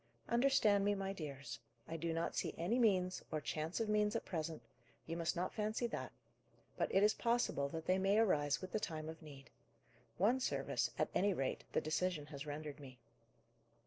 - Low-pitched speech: No, medium, 175 Hz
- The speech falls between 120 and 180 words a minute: No, average, 190 wpm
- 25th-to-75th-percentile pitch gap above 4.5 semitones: Yes, average, 5.3 semitones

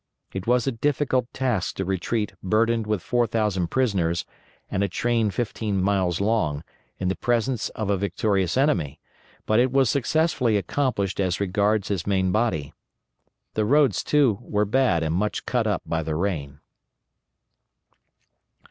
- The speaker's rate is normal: Yes, average, 150 wpm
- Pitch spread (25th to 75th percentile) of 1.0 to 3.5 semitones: No, average, 4.4 semitones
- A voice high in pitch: No, low, 105 Hz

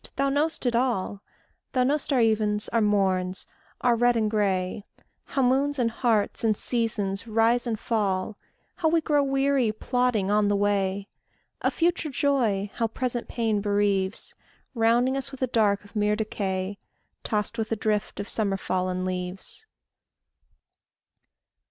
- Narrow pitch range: No, average, 3.7 semitones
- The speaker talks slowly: No, average, 150 wpm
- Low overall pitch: No, high, 220 Hz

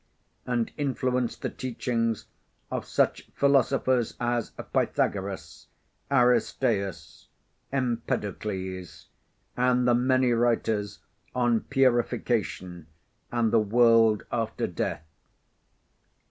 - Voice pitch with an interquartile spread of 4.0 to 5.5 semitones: No, average, 2.7 semitones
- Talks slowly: Yes, slow, 80 wpm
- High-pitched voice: No, low, 120 Hz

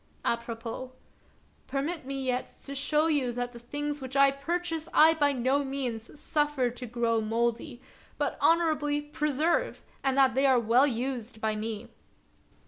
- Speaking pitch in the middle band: No, very high, 270 Hz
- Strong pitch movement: No, average, 3.6 semitones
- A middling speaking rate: Yes, average, 155 wpm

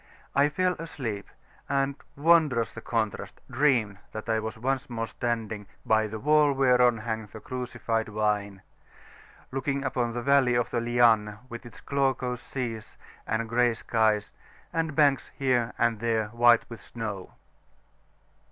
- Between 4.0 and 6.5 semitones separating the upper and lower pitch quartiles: No, average, 3.3 semitones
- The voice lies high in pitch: No, low, 120 Hz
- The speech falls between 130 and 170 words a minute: Yes, average, 145 wpm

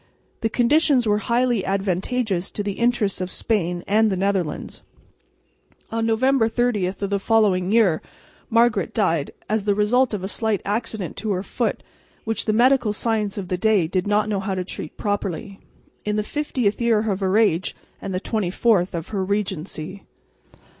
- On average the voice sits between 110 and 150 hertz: No, high, 205 Hz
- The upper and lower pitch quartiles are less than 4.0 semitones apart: Yes, average, 3.0 semitones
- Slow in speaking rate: No, average, 170 wpm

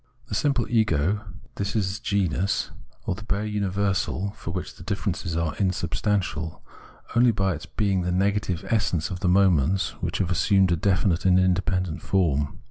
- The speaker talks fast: No, average, 160 wpm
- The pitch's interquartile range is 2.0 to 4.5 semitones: Yes, narrow, 2.4 semitones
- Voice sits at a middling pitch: No, very low, 95 Hz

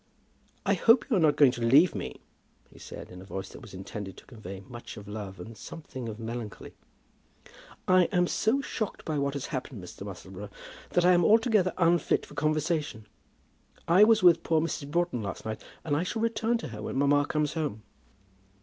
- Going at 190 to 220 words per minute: Yes, average, 195 wpm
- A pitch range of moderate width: No, wide, 8.2 semitones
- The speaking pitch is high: No, medium, 145 Hz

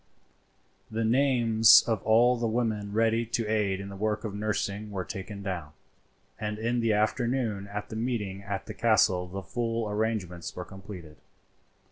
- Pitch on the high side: No, low, 105 Hz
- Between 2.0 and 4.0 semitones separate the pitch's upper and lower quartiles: Yes, narrow, 2.5 semitones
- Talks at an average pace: Yes, average, 160 wpm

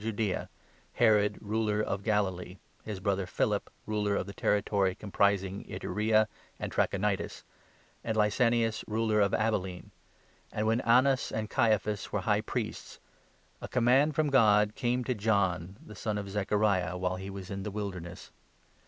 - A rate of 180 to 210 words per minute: No, average, 150 wpm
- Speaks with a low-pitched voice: Yes, low, 105 Hz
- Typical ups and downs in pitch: No, narrow, 2.1 semitones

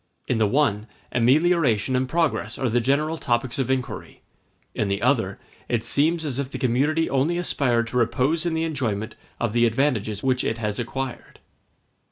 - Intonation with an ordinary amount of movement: Yes, average, 4.0 semitones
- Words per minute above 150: Yes, average, 175 wpm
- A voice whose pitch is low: Yes, low, 130 Hz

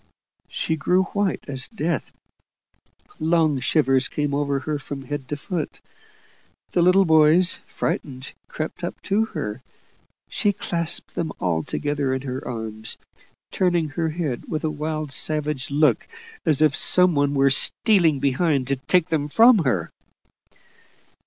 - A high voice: No, medium, 150 Hz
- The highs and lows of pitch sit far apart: No, average, 3.8 semitones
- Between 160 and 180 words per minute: No, average, 140 wpm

